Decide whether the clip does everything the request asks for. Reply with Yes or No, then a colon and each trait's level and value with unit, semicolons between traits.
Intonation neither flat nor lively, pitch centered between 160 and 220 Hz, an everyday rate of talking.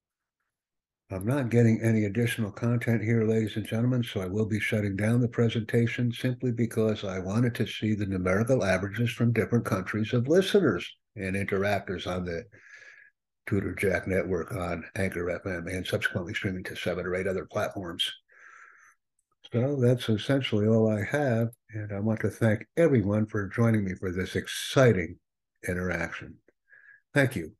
No: average, 3.5 semitones; low, 110 Hz; average, 155 wpm